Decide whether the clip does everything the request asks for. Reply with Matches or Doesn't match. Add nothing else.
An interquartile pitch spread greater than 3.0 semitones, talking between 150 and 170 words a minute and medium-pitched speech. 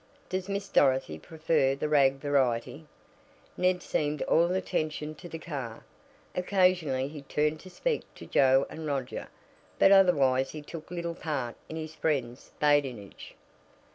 Doesn't match